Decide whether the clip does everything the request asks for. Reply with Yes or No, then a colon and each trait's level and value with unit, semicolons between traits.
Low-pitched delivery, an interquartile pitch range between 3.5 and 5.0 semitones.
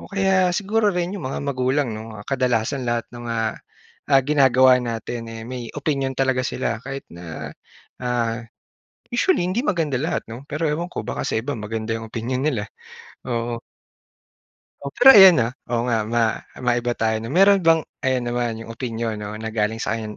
Yes: low, 125 Hz; average, 4.3 semitones